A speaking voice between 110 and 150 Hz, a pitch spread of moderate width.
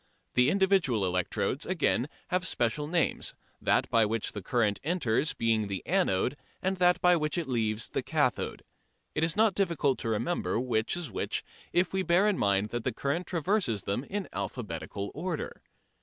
No: medium, 140 Hz; wide, 8.3 semitones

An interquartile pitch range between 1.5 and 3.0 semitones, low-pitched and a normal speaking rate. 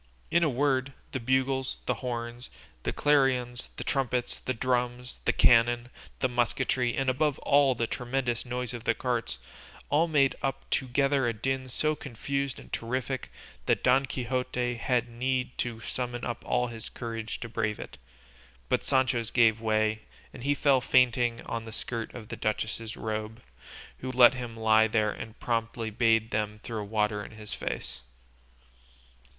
Yes: narrow, 2.4 semitones; low, 120 Hz; average, 160 wpm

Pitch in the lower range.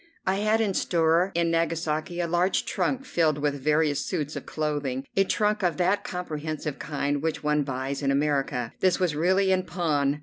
No: medium, 160 Hz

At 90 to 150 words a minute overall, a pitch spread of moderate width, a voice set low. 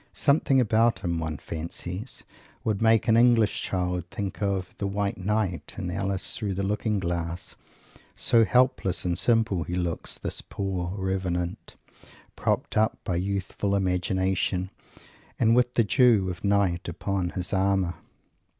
Yes: average, 140 wpm; average, 3.0 semitones; very low, 95 Hz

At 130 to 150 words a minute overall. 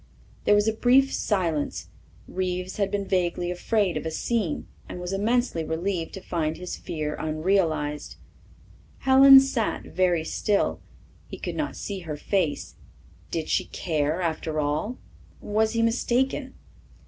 Yes: average, 140 wpm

